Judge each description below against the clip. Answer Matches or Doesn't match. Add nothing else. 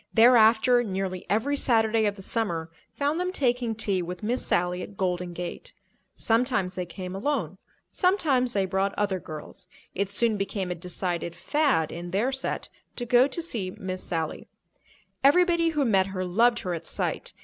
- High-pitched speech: Matches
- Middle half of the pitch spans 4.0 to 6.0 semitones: Matches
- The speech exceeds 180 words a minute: Doesn't match